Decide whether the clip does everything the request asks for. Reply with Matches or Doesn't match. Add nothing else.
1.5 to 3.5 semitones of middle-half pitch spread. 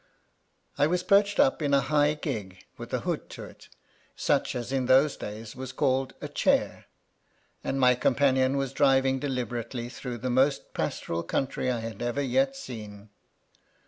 Matches